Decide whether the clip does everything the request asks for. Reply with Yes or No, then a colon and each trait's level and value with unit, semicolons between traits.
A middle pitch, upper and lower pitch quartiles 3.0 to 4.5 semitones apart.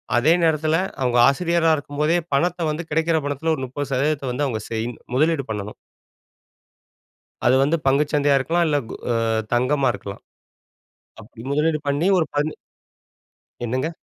Yes: medium, 145 Hz; average, 3.5 semitones